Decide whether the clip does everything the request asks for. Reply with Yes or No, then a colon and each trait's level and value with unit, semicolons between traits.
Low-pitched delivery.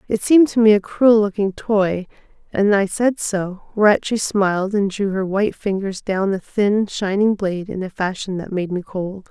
No: high, 200 Hz